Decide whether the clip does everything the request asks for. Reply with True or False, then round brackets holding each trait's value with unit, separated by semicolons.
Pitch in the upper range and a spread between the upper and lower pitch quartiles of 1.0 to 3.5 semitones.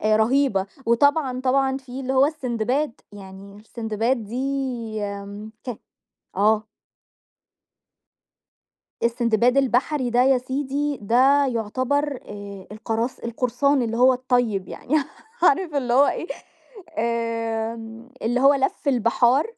True (245 Hz; 3.2 semitones)